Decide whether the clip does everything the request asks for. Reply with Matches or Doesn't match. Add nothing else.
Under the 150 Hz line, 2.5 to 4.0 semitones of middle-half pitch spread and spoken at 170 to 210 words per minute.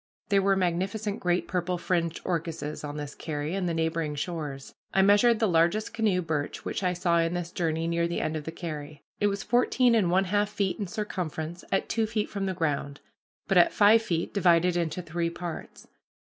Doesn't match